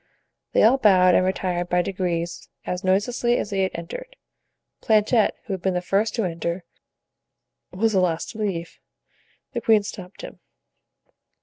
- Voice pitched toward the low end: No, high, 190 Hz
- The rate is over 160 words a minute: No, average, 155 wpm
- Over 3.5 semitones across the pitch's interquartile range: No, average, 3.2 semitones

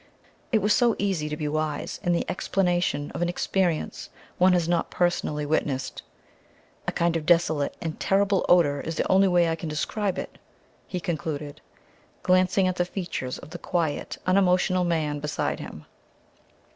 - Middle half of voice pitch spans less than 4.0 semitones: Yes, average, 3.2 semitones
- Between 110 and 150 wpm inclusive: No, average, 165 wpm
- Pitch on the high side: No, medium, 175 Hz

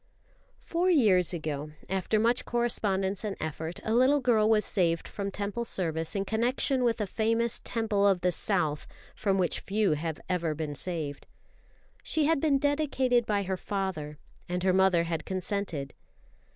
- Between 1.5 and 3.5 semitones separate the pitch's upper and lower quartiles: No, average, 5.2 semitones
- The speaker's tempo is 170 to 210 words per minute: No, average, 160 wpm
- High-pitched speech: Yes, high, 195 Hz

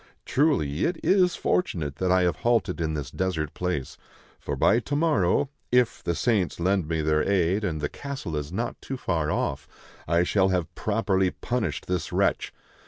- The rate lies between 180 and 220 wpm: Yes, average, 185 wpm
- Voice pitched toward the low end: Yes, very low, 90 Hz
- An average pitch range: No, wide, 6.7 semitones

